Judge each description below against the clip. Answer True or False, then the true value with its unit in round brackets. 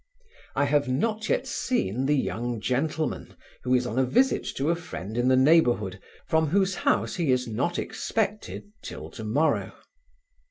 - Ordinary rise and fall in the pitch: False (5.7 semitones)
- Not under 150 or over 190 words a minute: True (165 wpm)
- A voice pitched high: False (140 Hz)